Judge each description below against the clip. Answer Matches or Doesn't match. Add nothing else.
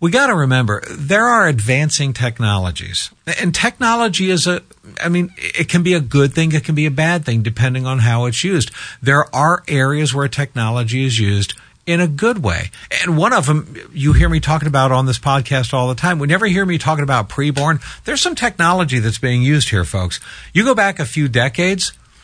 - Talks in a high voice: Doesn't match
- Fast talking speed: Matches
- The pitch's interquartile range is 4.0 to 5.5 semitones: Matches